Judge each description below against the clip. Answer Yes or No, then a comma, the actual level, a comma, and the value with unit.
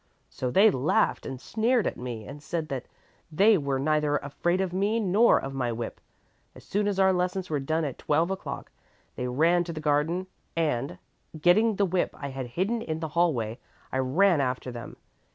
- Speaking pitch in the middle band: Yes, medium, 155 Hz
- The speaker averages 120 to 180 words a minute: No, average, 190 wpm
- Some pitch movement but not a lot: No, wide, 5.7 semitones